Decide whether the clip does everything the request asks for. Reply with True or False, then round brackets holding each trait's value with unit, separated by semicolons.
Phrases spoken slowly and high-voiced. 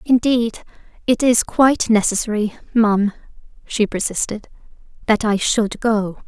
True (115 wpm; 220 Hz)